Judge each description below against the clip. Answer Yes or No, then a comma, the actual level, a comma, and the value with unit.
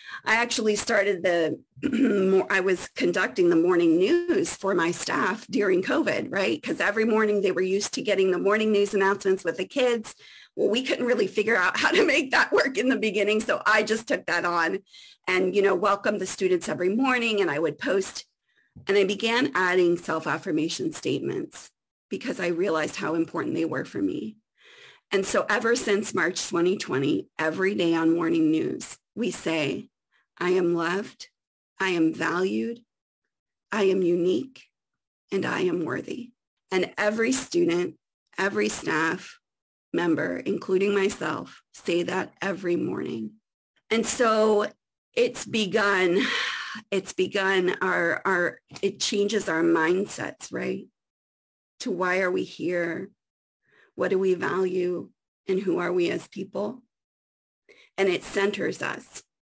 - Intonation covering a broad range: No, average, 4.1 semitones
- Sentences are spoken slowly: No, average, 150 wpm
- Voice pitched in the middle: No, high, 195 Hz